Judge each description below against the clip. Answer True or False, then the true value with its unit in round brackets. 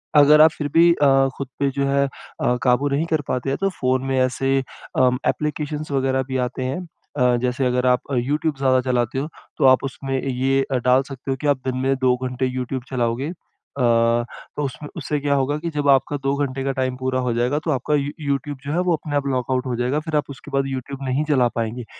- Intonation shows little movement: True (2.1 semitones)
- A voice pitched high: False (135 Hz)